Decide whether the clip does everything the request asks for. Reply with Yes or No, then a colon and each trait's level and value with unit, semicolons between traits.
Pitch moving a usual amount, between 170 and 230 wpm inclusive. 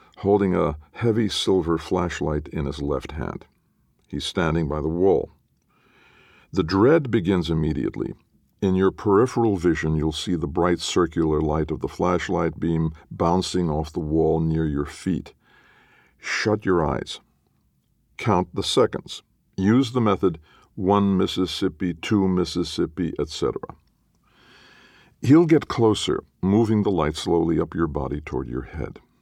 No: average, 3.9 semitones; slow, 135 wpm